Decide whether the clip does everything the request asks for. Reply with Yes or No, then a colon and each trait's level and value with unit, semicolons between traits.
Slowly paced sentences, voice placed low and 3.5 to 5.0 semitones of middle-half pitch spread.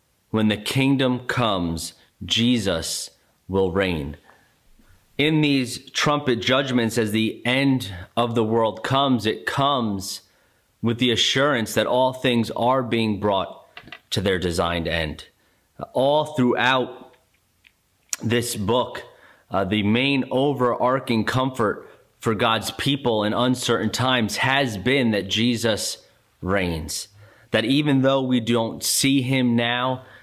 Yes: slow, 120 wpm; low, 120 Hz; average, 4.0 semitones